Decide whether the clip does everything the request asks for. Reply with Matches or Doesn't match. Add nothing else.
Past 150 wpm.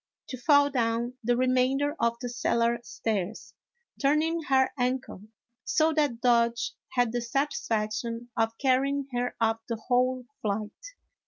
Doesn't match